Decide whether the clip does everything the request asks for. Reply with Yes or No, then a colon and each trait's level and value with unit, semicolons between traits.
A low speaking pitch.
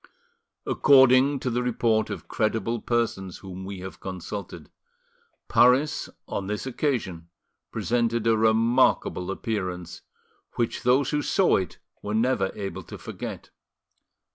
Yes: low, 115 Hz